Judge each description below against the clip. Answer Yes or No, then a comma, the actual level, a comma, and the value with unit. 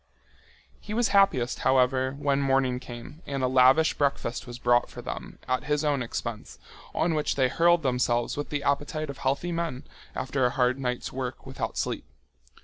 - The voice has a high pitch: No, low, 135 Hz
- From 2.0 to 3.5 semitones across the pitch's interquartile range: Yes, average, 2.8 semitones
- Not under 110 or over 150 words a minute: No, average, 175 wpm